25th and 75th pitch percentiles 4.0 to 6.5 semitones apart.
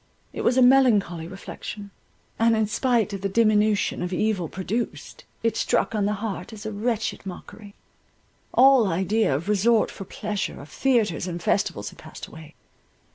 No: average, 3.3 semitones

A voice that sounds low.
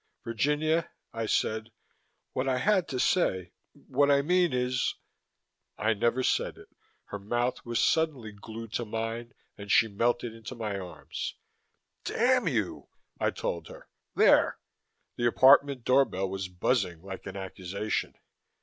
Yes: low, 115 Hz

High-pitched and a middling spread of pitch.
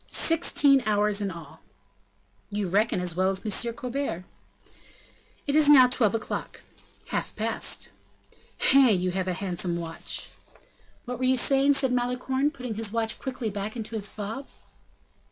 Yes: high, 225 Hz; average, 4.8 semitones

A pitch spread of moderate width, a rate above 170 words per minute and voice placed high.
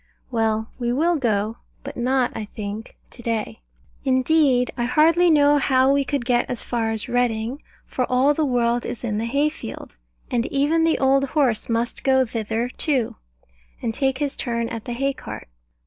Yes: average, 3.2 semitones; average, 180 wpm; very high, 250 Hz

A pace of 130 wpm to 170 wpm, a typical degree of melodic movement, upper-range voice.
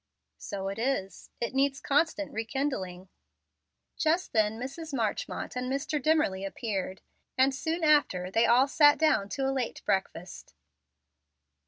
No: slow, 135 wpm; wide, 6.6 semitones; very high, 260 Hz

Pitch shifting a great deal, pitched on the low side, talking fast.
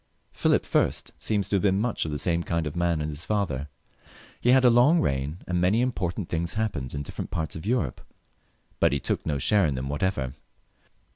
Yes: wide, 6.1 semitones; very low, 85 Hz; fast, 210 wpm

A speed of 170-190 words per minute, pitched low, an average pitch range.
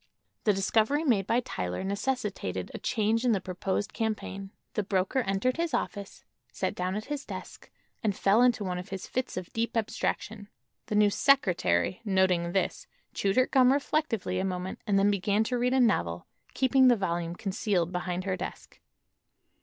No: average, 175 wpm; high, 200 Hz; average, 4.1 semitones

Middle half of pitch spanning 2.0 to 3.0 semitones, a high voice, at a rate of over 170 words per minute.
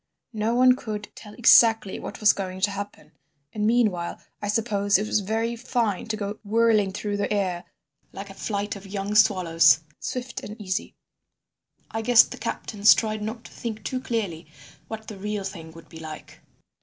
Yes: narrow, 2.4 semitones; high, 210 Hz; average, 180 wpm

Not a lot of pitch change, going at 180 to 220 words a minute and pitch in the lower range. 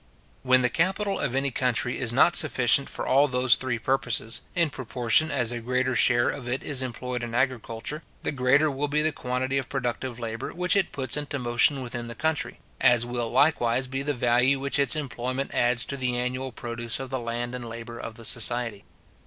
Yes: narrow, 2.3 semitones; average, 200 wpm; low, 125 Hz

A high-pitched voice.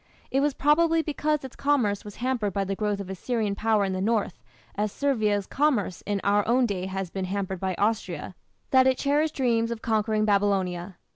Yes: high, 210 Hz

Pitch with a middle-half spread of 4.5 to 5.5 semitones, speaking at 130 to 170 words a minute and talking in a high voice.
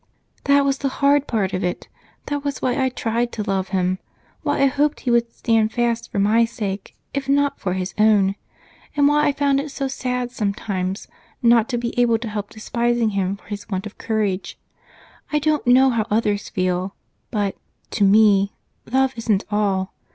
No: average, 4.8 semitones; average, 190 wpm; high, 225 Hz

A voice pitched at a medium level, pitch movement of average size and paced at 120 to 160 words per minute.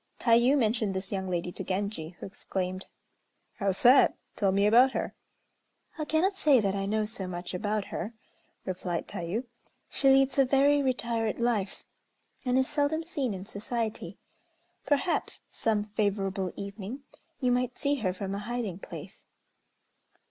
No: high, 215 Hz; average, 4.9 semitones; average, 155 wpm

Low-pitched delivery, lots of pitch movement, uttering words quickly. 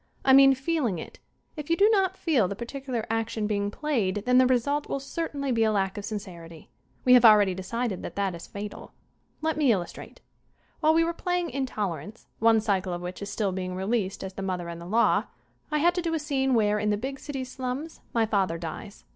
No: high, 225 Hz; wide, 6.0 semitones; fast, 220 wpm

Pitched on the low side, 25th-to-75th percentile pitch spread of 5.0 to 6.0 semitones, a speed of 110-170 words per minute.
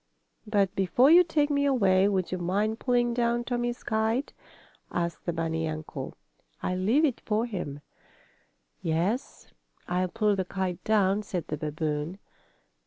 No: high, 200 Hz; average, 5.3 semitones; average, 145 wpm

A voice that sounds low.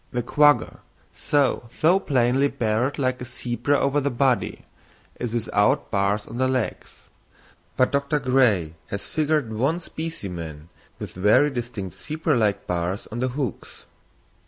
Yes: low, 125 Hz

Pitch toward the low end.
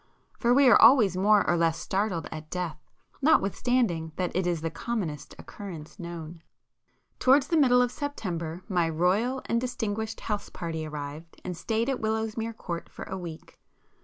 No: high, 190 Hz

